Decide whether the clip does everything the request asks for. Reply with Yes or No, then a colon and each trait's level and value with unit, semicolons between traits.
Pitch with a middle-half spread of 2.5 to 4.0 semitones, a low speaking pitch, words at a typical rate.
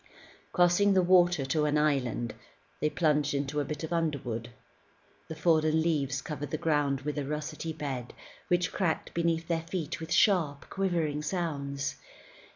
No: average, 2.9 semitones; medium, 155 Hz; average, 155 wpm